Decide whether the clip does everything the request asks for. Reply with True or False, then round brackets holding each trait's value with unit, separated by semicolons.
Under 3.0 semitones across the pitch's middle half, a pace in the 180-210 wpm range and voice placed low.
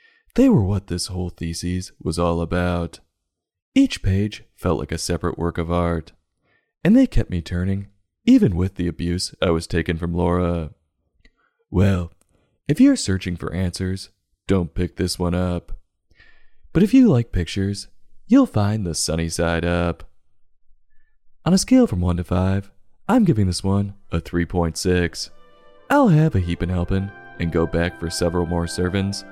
False (2.5 semitones; 165 wpm; 90 Hz)